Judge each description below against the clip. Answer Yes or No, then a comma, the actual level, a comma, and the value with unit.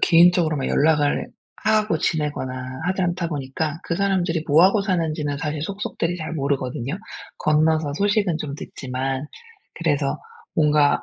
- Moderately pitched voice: Yes, medium, 155 Hz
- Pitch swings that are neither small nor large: Yes, average, 3.4 semitones